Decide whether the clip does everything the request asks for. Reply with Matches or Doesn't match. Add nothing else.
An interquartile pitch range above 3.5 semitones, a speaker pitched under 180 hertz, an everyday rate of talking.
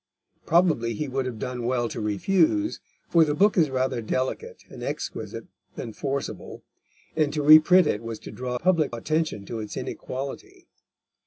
Matches